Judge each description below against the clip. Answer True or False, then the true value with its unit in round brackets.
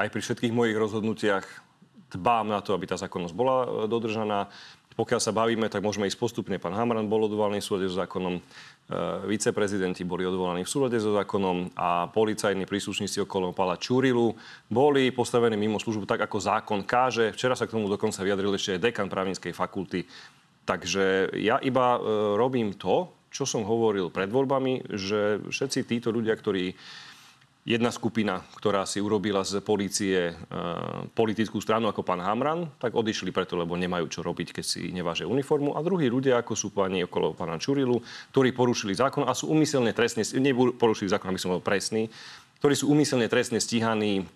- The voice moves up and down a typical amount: True (3.8 semitones)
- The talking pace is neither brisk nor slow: False (170 wpm)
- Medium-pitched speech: False (110 Hz)